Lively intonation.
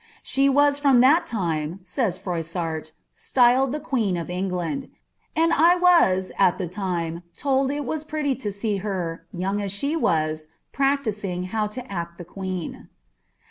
Yes: wide, 7.4 semitones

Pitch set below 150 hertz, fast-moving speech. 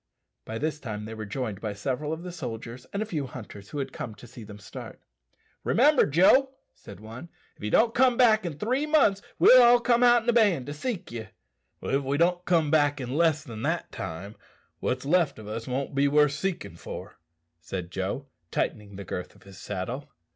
Yes: medium, 140 Hz; fast, 210 wpm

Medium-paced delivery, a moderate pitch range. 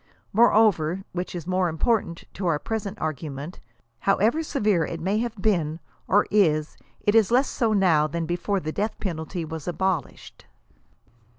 Yes: average, 170 wpm; average, 4.6 semitones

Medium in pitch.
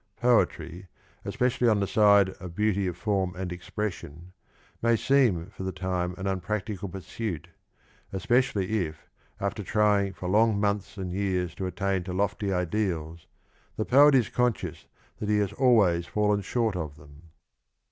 No: low, 100 Hz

